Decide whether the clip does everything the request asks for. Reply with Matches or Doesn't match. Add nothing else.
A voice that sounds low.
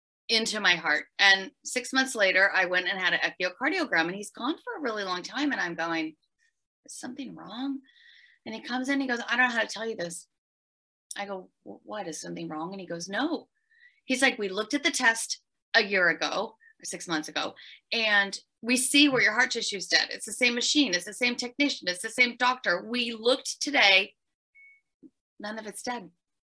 Doesn't match